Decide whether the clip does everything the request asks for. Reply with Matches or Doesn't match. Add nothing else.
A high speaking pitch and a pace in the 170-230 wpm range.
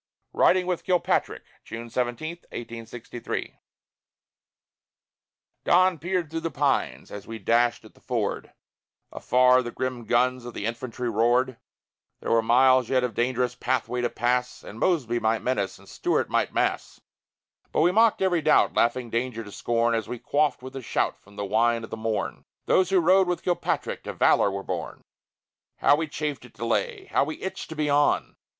Doesn't match